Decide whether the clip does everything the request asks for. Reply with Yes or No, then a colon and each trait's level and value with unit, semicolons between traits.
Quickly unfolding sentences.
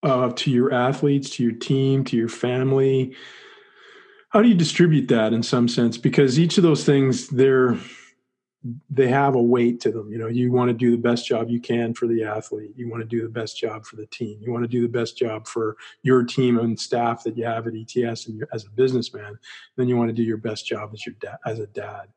Yes: fast, 245 wpm